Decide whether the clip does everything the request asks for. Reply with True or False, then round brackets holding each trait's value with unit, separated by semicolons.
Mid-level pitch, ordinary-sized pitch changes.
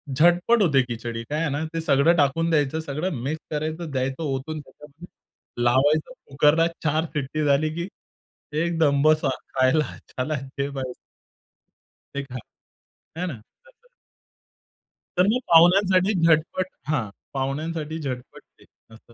True (150 Hz; 3.3 semitones)